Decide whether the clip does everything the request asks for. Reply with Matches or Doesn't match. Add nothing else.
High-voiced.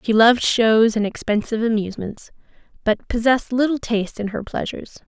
Matches